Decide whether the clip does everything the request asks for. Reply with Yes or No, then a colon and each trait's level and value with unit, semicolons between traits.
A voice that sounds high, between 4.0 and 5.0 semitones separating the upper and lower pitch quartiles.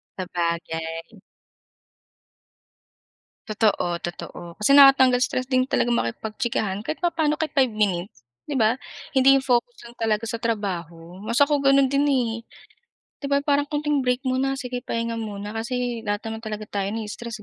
Yes: high, 230 Hz; average, 4.6 semitones